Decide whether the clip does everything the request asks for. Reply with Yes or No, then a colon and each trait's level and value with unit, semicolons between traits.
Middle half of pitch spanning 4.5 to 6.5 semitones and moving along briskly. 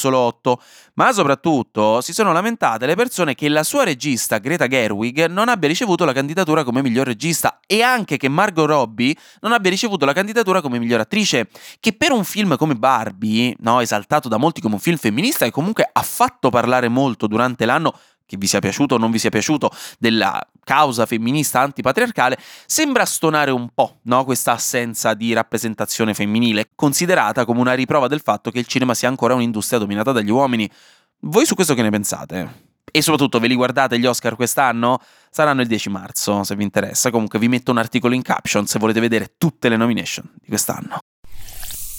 Yes: wide, 5.4 semitones; fast, 185 wpm